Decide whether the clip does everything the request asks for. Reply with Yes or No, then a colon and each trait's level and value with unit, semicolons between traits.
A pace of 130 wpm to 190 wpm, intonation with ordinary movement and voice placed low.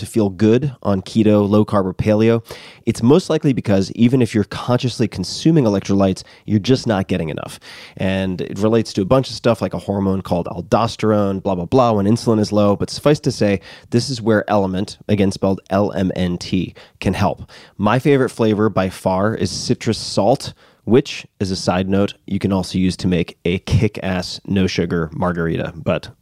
Yes: average, 185 wpm; average, 3.2 semitones; low, 100 Hz